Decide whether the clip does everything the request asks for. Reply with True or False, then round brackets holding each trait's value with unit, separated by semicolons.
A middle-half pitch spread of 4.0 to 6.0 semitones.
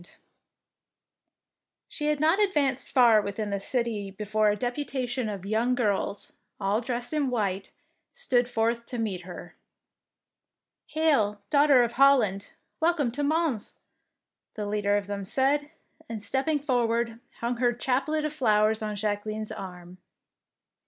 True (4.8 semitones)